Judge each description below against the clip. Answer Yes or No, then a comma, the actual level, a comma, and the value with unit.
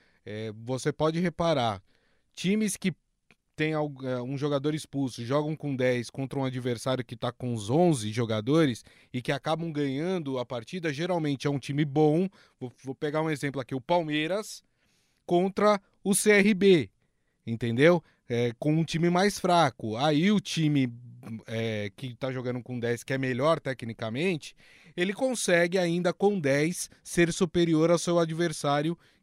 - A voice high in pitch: No, medium, 150 Hz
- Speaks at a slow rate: No, average, 145 wpm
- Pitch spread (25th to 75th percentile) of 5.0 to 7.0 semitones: Yes, wide, 5.4 semitones